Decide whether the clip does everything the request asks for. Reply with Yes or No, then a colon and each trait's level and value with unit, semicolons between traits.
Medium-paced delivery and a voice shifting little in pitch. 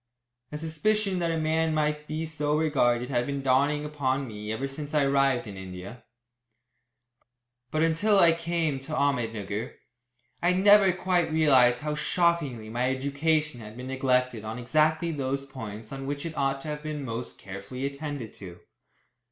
No: average, 165 wpm; average, 4.1 semitones